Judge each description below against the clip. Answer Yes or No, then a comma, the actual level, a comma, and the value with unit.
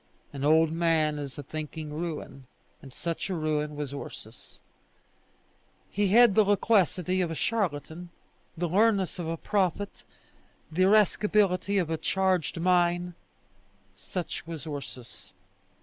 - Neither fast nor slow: No, slow, 130 wpm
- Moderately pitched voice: Yes, medium, 170 Hz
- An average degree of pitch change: Yes, average, 3.8 semitones